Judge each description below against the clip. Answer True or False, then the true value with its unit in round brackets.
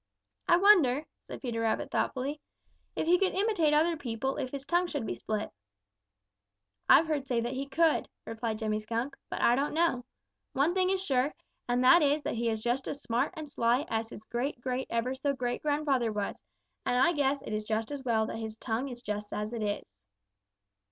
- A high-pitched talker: True (260 Hz)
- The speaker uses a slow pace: False (205 wpm)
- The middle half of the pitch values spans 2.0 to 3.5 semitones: False (4.6 semitones)